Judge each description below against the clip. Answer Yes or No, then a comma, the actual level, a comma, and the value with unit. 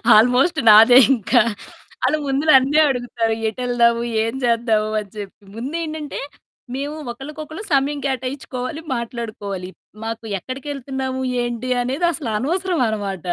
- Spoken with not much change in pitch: No, average, 3.8 semitones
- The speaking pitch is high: Yes, very high, 255 Hz